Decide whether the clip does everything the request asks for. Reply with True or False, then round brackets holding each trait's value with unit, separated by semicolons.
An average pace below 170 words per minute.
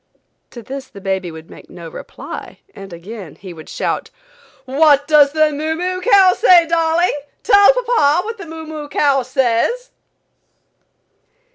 True (150 wpm)